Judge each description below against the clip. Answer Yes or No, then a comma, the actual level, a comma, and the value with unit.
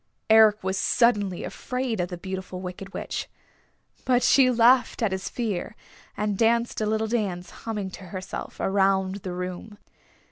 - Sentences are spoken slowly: No, average, 150 wpm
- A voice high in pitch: Yes, high, 200 Hz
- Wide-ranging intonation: No, average, 3.2 semitones